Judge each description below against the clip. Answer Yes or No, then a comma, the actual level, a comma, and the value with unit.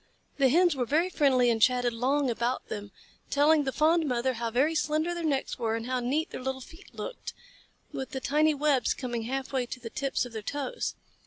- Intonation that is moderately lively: Yes, average, 3.7 semitones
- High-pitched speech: Yes, very high, 265 Hz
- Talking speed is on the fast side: Yes, fast, 215 wpm